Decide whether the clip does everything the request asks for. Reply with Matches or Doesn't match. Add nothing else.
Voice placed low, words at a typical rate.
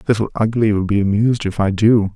Doesn't match